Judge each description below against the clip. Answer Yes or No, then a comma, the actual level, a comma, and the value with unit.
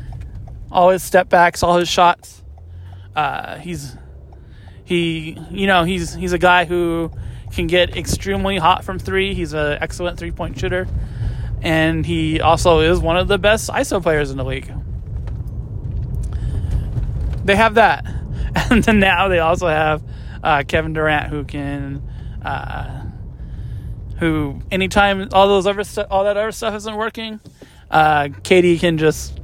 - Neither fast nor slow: Yes, average, 145 wpm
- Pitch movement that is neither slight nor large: No, wide, 7.7 semitones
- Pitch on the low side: No, medium, 160 Hz